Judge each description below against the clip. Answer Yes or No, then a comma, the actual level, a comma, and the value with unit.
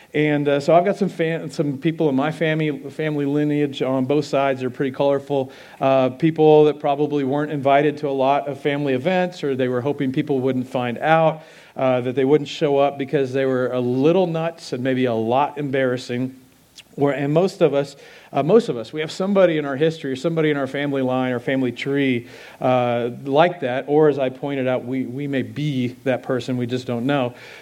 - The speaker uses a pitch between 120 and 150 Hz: Yes, medium, 140 Hz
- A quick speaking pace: Yes, fast, 215 wpm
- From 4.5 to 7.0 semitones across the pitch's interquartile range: No, average, 2.7 semitones